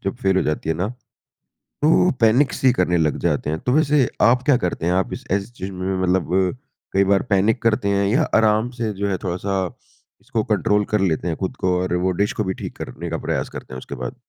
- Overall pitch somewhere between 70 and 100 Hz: Yes, very low, 95 Hz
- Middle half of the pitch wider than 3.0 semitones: Yes, average, 3.8 semitones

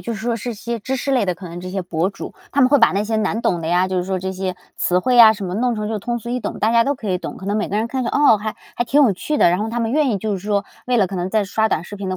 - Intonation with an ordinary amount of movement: Yes, average, 4.0 semitones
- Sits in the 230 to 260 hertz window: No, high, 215 Hz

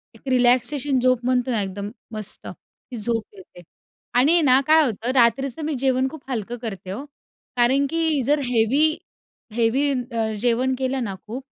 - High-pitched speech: Yes, very high, 250 Hz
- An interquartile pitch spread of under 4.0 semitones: Yes, average, 3.0 semitones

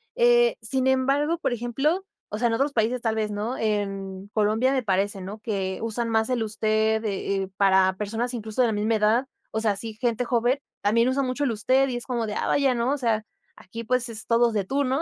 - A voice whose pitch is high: Yes, high, 230 Hz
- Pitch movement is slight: No, average, 3.2 semitones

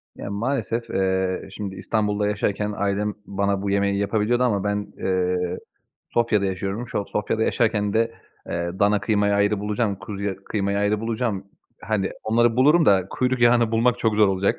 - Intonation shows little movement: Yes, narrow, 2.3 semitones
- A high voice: No, low, 105 Hz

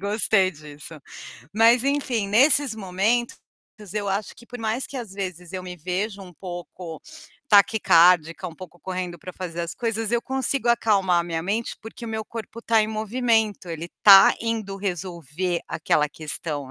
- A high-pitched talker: Yes, high, 195 Hz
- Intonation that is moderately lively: Yes, average, 4.4 semitones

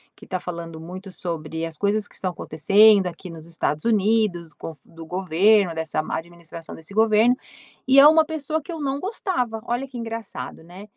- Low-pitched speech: No, high, 195 Hz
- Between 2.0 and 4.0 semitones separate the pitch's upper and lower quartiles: No, wide, 5.6 semitones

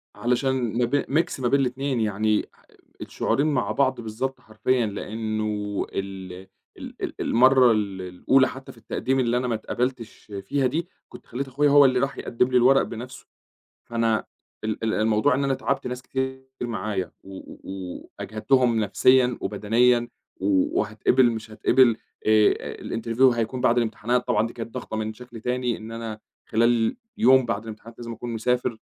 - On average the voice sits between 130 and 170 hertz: No, low, 120 Hz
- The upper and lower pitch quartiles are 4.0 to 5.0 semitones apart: No, average, 2.9 semitones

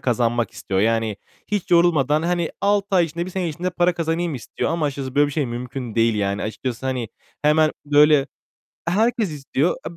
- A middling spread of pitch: No, wide, 6.0 semitones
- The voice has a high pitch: No, medium, 150 Hz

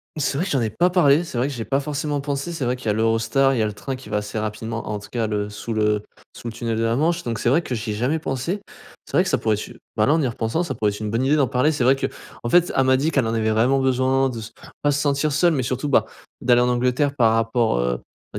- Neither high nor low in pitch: No, low, 125 Hz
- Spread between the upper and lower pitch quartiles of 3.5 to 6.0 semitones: Yes, average, 4.0 semitones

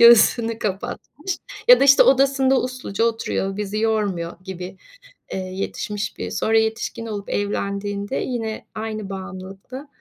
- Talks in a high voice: Yes, high, 215 Hz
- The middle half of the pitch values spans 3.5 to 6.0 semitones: No, average, 3.1 semitones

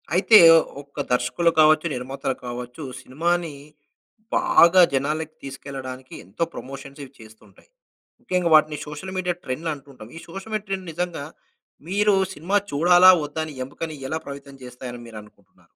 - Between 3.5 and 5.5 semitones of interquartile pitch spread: Yes, average, 4.9 semitones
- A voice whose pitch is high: No, medium, 150 Hz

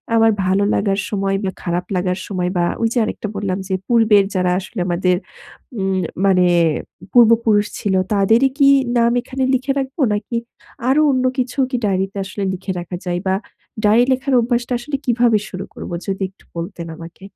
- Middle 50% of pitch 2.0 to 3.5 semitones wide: No, average, 4.2 semitones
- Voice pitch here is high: Yes, high, 205 Hz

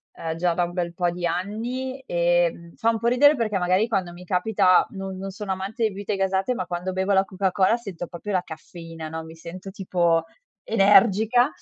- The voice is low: No, high, 190 Hz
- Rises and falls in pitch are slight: No, average, 3.3 semitones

